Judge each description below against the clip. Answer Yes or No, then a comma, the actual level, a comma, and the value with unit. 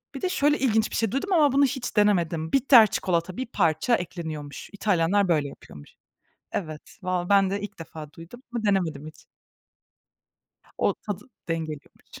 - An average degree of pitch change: No, wide, 5.9 semitones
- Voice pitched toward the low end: No, high, 190 Hz